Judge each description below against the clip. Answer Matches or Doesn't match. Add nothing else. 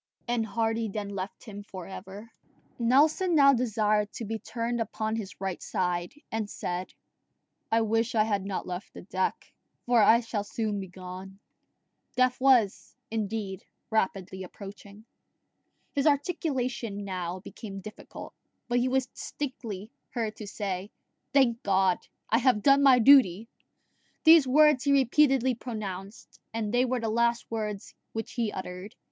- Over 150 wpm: Doesn't match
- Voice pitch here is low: Doesn't match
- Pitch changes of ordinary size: Matches